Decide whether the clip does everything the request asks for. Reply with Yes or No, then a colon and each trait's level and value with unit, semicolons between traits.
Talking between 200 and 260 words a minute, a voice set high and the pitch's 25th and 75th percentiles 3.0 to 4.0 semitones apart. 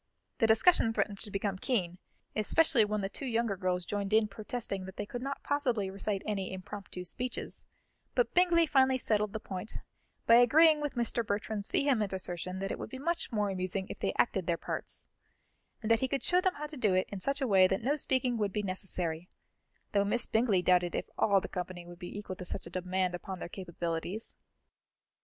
No: fast, 205 wpm; high, 205 Hz; average, 4.7 semitones